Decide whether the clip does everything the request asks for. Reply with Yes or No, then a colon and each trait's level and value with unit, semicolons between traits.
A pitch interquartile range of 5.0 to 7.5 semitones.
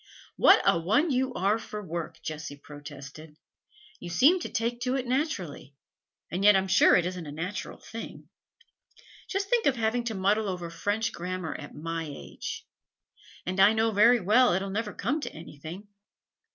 Yes: wide, 5.6 semitones